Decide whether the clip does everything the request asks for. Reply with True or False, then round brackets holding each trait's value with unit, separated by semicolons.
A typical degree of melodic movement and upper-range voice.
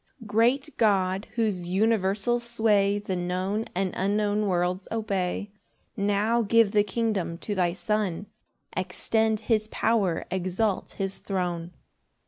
True (3.0 semitones; 205 Hz)